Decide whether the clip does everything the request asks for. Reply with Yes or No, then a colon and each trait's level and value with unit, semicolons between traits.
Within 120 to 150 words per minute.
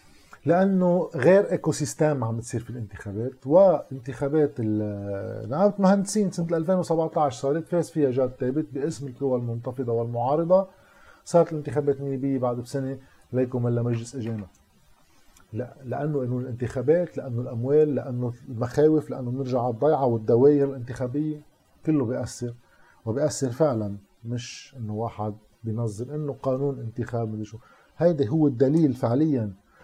Yes: average, 125 wpm